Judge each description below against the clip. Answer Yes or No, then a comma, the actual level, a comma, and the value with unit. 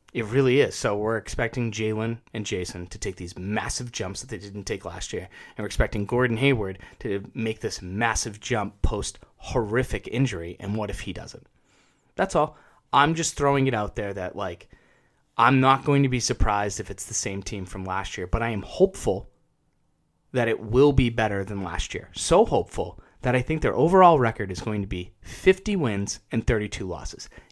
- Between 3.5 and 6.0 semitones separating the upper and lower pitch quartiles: Yes, average, 4.1 semitones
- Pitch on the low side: Yes, low, 110 Hz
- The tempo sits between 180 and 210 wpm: Yes, average, 200 wpm